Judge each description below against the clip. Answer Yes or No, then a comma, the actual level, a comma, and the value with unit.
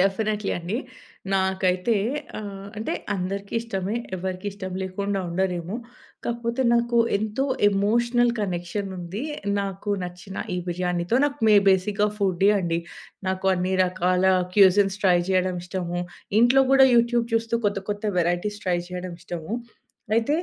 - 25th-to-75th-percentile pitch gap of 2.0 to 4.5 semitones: Yes, average, 2.9 semitones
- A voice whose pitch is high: Yes, high, 195 Hz